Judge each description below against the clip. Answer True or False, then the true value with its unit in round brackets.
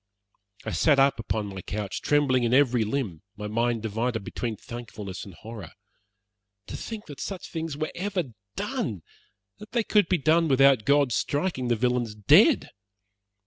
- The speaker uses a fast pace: False (160 wpm)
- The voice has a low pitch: True (125 Hz)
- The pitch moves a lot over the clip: True (5.8 semitones)